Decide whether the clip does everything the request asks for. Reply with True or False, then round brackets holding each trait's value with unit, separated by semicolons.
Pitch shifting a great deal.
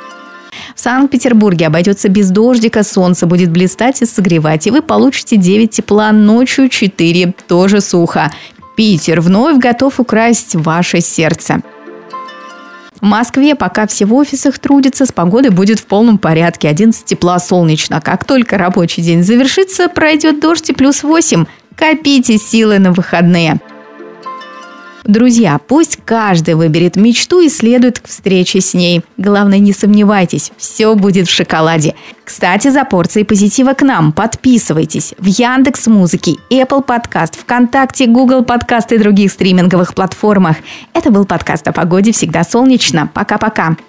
True (5.7 semitones)